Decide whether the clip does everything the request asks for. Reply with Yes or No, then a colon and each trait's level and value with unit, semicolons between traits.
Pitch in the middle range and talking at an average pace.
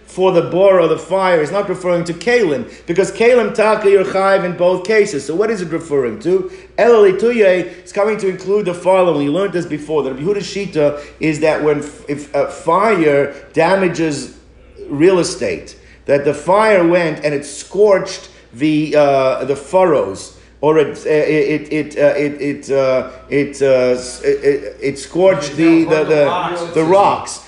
Yes: medium, 175 Hz; average, 145 wpm